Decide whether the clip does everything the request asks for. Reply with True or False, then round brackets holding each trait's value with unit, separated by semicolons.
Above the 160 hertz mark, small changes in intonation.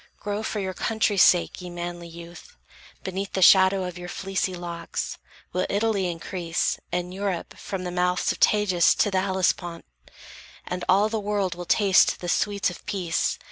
True (185 Hz; 2.2 semitones)